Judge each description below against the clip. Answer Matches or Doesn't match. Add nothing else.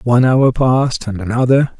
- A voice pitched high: Doesn't match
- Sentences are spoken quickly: Doesn't match